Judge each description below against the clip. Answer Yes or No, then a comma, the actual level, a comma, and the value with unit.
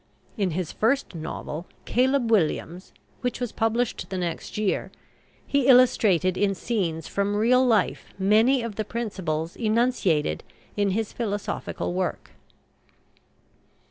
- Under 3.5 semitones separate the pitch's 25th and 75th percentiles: No, average, 4.5 semitones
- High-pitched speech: Yes, high, 210 Hz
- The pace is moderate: No, slow, 120 wpm